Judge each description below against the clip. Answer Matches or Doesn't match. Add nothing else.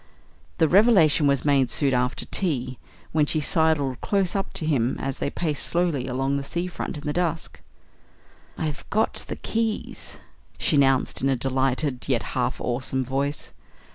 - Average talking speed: Matches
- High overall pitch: Doesn't match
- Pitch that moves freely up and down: Doesn't match